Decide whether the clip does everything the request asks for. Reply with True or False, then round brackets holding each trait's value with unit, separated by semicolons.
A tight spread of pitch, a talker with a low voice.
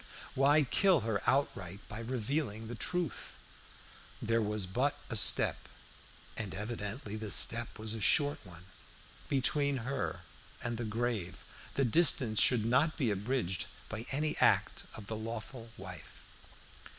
False (4.2 semitones; 115 Hz)